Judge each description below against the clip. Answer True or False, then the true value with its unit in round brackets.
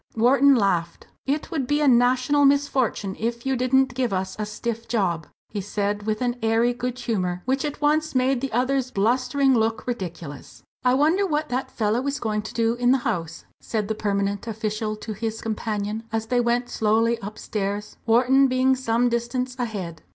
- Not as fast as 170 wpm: False (180 wpm)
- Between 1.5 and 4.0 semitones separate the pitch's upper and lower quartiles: True (3.4 semitones)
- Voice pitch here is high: True (235 Hz)